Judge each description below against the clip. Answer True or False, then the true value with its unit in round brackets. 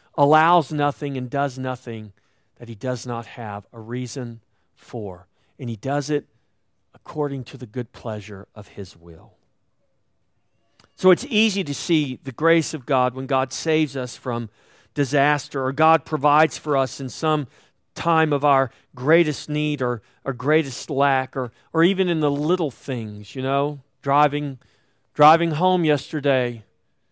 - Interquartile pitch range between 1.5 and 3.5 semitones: False (4.2 semitones)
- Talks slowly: False (155 wpm)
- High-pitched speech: False (135 Hz)